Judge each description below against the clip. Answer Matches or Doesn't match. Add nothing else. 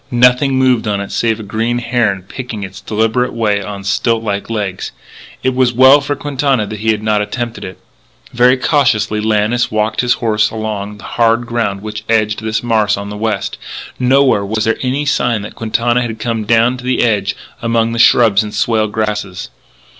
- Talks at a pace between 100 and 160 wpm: Doesn't match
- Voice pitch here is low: Matches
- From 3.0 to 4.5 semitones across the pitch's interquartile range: Doesn't match